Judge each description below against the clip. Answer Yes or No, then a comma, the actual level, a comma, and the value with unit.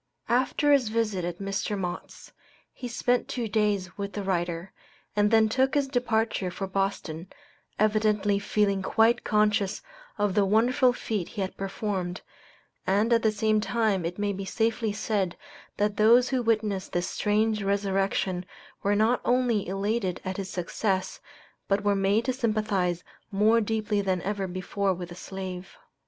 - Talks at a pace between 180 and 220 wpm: No, average, 155 wpm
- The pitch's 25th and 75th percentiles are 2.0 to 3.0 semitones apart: Yes, narrow, 2.5 semitones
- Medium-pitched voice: No, high, 205 Hz